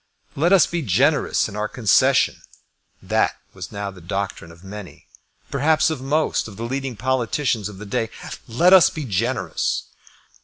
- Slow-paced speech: No, average, 160 wpm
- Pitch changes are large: Yes, wide, 6.3 semitones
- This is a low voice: Yes, low, 120 Hz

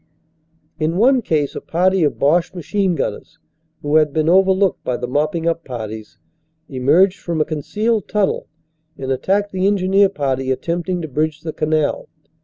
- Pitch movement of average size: Yes, average, 4.5 semitones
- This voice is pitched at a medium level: Yes, medium, 165 Hz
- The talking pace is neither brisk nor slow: Yes, average, 160 wpm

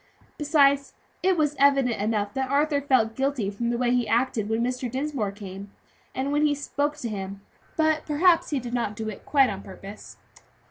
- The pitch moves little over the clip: No, average, 4.9 semitones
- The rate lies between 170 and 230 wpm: Yes, average, 190 wpm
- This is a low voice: No, very high, 255 Hz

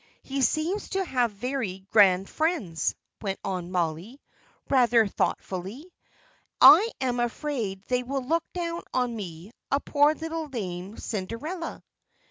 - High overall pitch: Yes, high, 245 Hz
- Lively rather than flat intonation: Yes, wide, 7.6 semitones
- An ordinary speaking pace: No, slow, 125 wpm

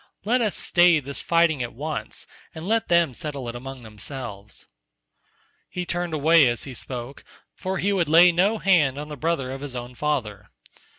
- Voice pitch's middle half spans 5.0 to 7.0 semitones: Yes, average, 5.3 semitones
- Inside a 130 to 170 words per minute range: No, average, 180 wpm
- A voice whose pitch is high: No, medium, 150 Hz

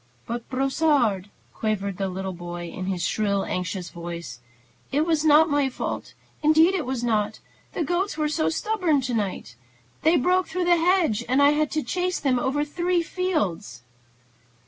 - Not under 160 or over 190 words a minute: Yes, average, 165 wpm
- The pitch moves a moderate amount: No, wide, 8.3 semitones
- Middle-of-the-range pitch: No, very high, 275 Hz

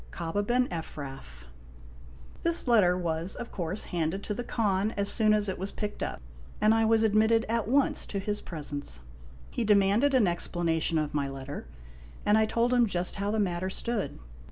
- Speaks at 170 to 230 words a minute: Yes, average, 180 wpm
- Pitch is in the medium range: No, high, 200 Hz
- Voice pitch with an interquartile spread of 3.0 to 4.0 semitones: No, average, 4.6 semitones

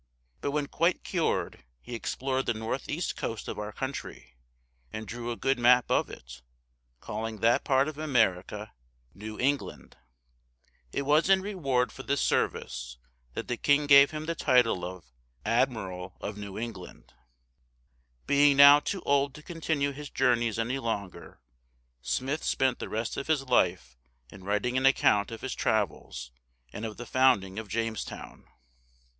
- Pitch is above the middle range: No, low, 125 Hz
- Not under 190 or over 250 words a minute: No, average, 155 wpm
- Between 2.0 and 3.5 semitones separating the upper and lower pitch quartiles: No, average, 5.0 semitones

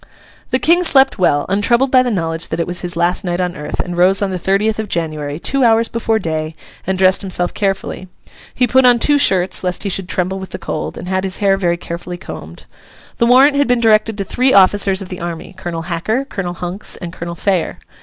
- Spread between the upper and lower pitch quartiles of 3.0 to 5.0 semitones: Yes, average, 4.2 semitones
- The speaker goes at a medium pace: No, fast, 225 wpm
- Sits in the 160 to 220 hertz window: Yes, high, 190 Hz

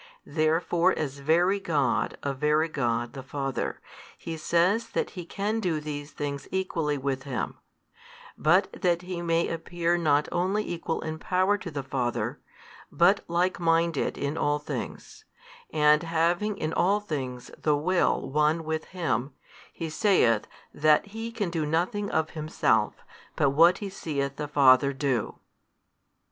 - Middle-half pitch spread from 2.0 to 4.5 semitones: Yes, average, 3.7 semitones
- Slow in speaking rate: No, average, 145 wpm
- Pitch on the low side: No, medium, 160 Hz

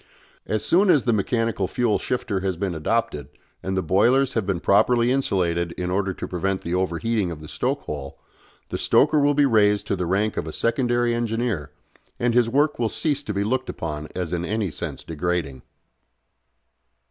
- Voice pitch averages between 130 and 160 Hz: No, low, 105 Hz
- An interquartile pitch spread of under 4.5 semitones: No, average, 5.3 semitones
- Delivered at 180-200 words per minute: Yes, average, 185 wpm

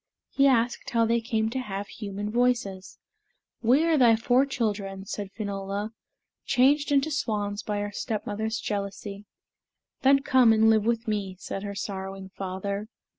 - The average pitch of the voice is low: No, high, 215 Hz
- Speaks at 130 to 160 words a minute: Yes, average, 150 wpm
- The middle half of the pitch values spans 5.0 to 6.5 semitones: No, average, 3.2 semitones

